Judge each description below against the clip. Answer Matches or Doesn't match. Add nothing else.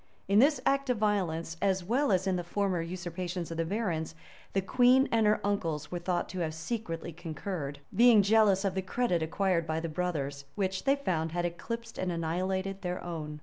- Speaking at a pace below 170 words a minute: Doesn't match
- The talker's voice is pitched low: Doesn't match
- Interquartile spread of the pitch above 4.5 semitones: Doesn't match